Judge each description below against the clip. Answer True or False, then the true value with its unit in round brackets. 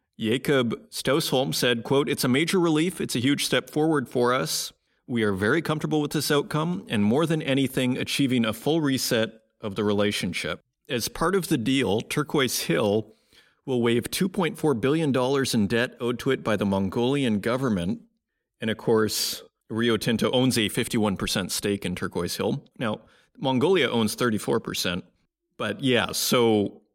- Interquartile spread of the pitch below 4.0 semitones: False (4.7 semitones)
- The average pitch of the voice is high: False (125 Hz)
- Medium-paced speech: True (175 wpm)